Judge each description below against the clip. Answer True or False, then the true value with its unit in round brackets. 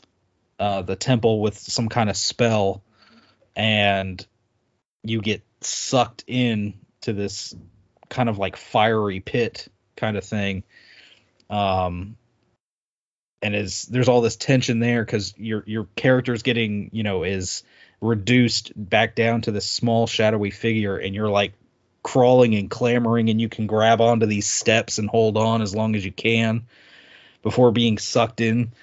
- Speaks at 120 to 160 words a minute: True (150 wpm)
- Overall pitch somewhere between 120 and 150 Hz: False (110 Hz)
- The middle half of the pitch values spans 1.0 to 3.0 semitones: True (2.4 semitones)